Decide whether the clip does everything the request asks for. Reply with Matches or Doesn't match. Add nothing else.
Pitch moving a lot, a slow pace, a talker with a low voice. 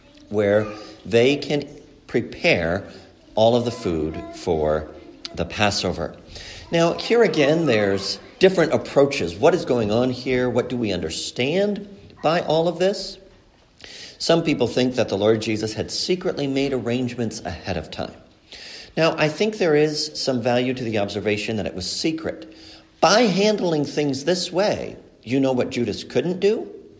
Doesn't match